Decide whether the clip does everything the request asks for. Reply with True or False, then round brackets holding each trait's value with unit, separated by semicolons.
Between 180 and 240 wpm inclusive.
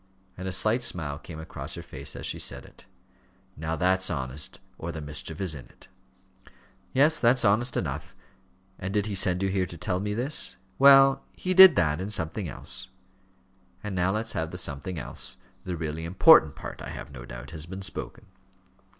True (190 wpm)